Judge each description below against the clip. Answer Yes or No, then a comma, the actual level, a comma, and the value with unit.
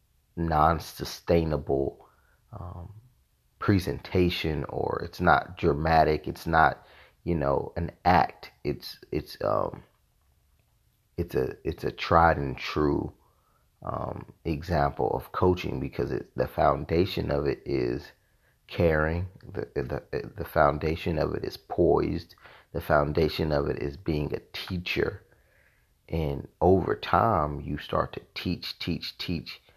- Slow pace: Yes, slow, 120 wpm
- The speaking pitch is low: Yes, very low, 80 Hz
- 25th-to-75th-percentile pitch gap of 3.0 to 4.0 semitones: Yes, average, 3.3 semitones